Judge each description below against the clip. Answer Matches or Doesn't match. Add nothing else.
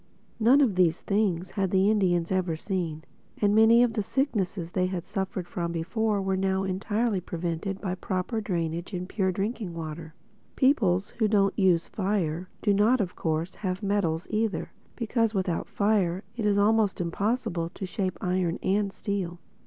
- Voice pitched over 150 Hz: Matches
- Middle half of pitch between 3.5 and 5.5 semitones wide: Doesn't match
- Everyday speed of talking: Matches